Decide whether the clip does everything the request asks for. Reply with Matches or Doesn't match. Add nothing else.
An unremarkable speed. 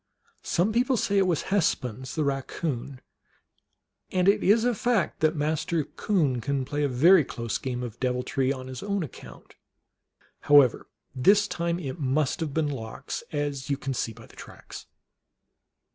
Matches